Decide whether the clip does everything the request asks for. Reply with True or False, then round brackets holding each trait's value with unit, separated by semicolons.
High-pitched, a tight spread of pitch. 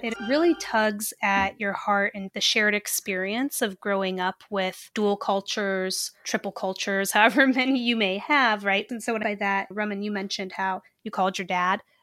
True (200 Hz; 2.2 semitones)